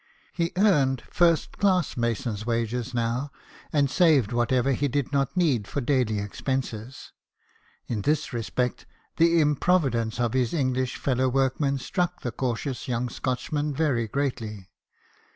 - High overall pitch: No, low, 130 Hz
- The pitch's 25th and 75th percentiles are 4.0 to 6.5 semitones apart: No, average, 3.6 semitones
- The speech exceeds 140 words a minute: No, slow, 135 wpm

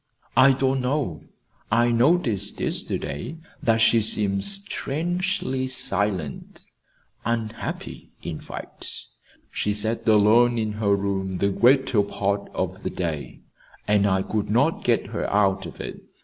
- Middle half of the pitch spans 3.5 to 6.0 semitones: Yes, average, 4.3 semitones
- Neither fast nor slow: No, slow, 130 wpm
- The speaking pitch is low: Yes, low, 110 Hz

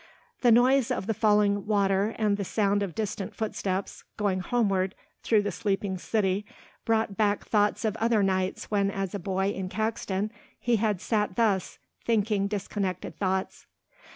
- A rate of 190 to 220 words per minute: No, average, 155 wpm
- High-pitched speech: Yes, high, 205 Hz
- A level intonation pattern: Yes, narrow, 2.1 semitones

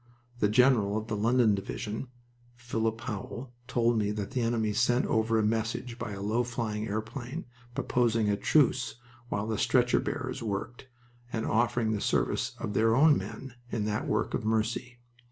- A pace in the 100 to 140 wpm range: No, average, 170 wpm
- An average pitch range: No, narrow, 2.3 semitones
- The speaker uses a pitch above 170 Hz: No, low, 115 Hz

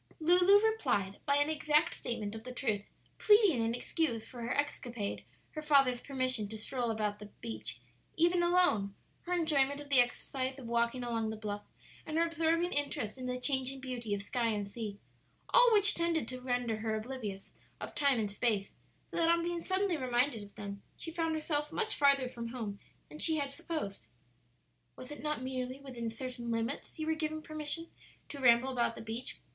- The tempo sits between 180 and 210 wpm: Yes, average, 190 wpm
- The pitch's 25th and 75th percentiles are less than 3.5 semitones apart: No, wide, 5.4 semitones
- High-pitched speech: Yes, very high, 255 Hz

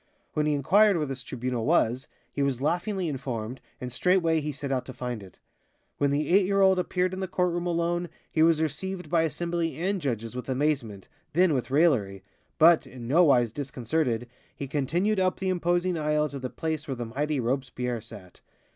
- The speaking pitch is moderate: Yes, medium, 150 Hz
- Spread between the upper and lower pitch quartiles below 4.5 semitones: No, wide, 5.4 semitones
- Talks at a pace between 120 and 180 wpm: No, average, 195 wpm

